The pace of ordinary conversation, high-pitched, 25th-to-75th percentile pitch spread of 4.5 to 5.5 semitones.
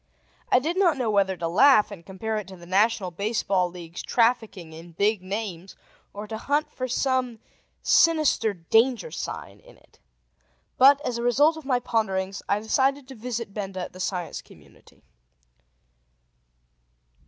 Yes: average, 155 wpm; high, 220 Hz; average, 5.2 semitones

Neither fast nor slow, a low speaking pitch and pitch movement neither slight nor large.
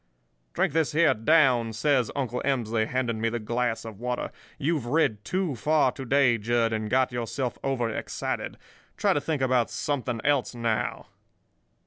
Yes: average, 160 wpm; low, 125 Hz; average, 3.6 semitones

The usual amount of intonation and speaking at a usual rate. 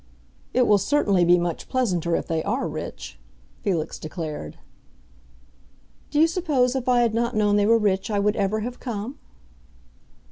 No: wide, 5.8 semitones; average, 165 wpm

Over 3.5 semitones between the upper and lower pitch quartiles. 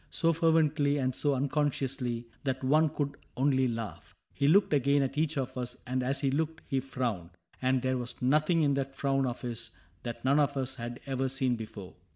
No: narrow, 2.4 semitones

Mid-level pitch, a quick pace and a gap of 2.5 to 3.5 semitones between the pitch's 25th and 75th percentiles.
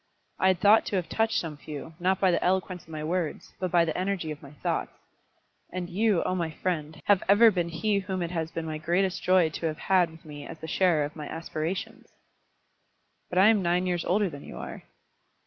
Yes: medium, 175 Hz; fast, 225 wpm; average, 2.8 semitones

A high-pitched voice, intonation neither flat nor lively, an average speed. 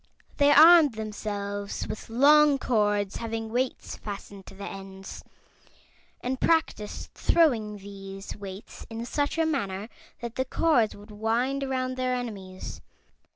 No: high, 225 Hz; average, 4.5 semitones; slow, 130 wpm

